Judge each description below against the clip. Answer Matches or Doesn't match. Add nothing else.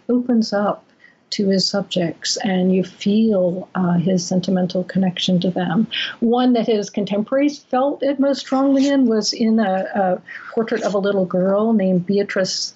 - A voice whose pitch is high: Matches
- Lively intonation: Doesn't match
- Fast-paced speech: Doesn't match